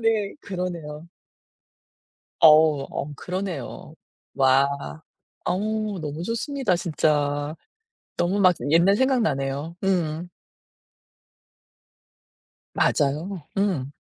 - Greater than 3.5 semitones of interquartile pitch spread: Yes, average, 5.3 semitones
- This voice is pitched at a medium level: Yes, medium, 170 Hz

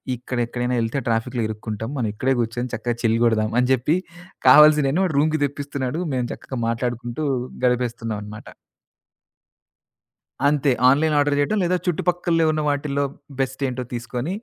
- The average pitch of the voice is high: No, low, 125 Hz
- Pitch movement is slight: No, average, 3.6 semitones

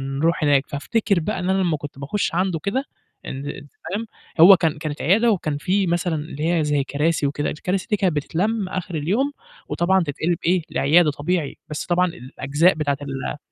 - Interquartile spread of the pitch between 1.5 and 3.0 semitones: No, average, 4.2 semitones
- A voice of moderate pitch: Yes, medium, 165 Hz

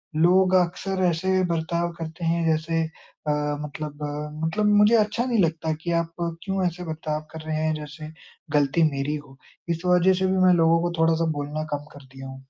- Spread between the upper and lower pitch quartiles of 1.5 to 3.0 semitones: Yes, narrow, 2.6 semitones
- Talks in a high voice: No, medium, 165 Hz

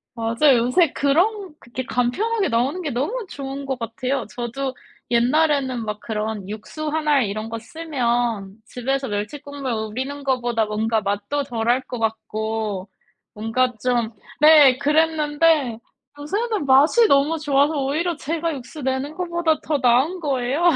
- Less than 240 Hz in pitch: No, very high, 265 Hz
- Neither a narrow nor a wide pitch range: Yes, average, 4.6 semitones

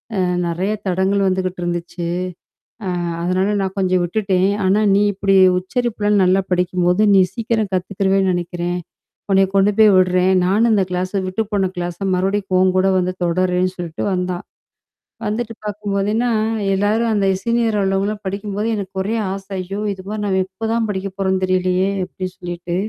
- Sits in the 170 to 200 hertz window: Yes, high, 190 Hz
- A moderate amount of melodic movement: No, narrow, 2.0 semitones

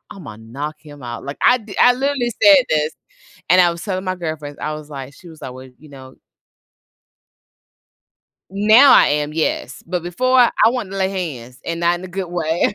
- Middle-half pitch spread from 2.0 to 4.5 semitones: No, average, 5.1 semitones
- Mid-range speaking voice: Yes, medium, 170 Hz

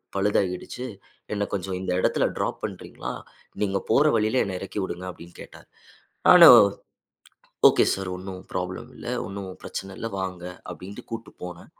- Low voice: Yes, very low, 95 Hz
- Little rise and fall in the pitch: Yes, narrow, 1.9 semitones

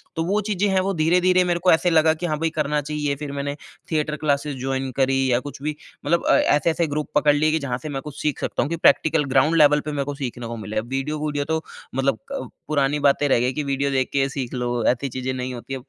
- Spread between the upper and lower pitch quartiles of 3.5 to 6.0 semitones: No, narrow, 2.6 semitones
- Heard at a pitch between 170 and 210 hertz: No, medium, 145 Hz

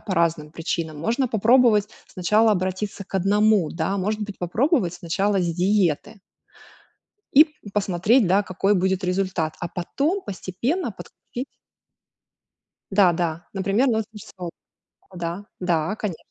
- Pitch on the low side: No, high, 195 Hz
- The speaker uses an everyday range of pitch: Yes, average, 3.4 semitones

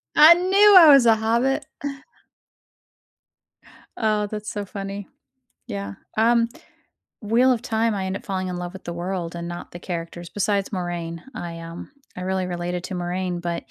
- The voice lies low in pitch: No, high, 190 Hz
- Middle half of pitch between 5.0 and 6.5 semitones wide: No, average, 4.1 semitones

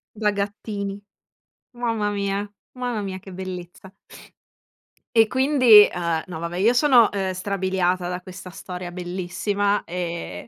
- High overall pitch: Yes, high, 195 Hz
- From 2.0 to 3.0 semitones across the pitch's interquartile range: Yes, narrow, 2.5 semitones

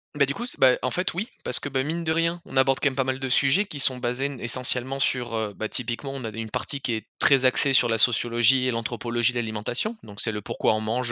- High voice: No, low, 130 Hz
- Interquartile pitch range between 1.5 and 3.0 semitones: Yes, average, 2.7 semitones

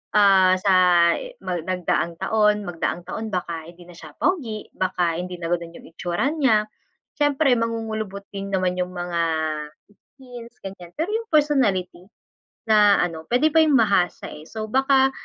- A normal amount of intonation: No, wide, 6.1 semitones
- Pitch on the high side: Yes, high, 200 Hz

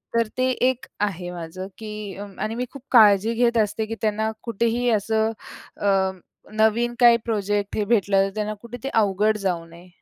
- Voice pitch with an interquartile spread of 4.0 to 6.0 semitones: No, average, 2.8 semitones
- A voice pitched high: Yes, high, 215 Hz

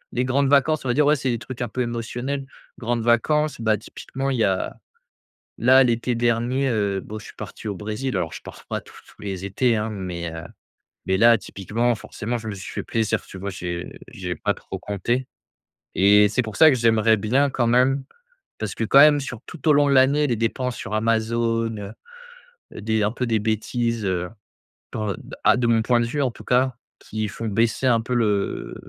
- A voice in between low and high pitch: No, low, 115 Hz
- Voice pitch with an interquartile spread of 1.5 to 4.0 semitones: Yes, average, 3.2 semitones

